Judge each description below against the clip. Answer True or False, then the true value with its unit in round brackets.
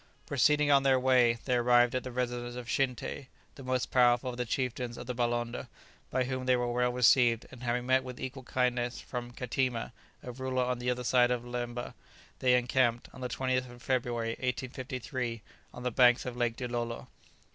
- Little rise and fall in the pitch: True (1.1 semitones)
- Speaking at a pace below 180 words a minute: False (195 wpm)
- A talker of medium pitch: False (125 Hz)